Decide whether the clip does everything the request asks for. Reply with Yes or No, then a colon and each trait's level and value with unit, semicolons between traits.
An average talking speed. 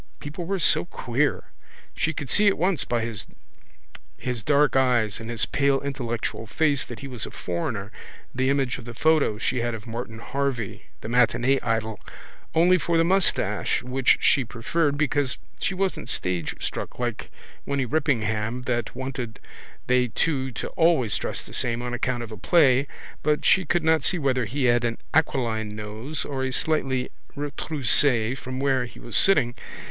Yes: average, 170 wpm